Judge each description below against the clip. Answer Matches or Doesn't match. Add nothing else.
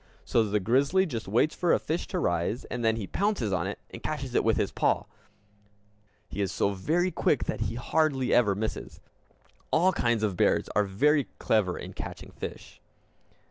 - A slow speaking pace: Doesn't match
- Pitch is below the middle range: Matches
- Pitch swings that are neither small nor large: Doesn't match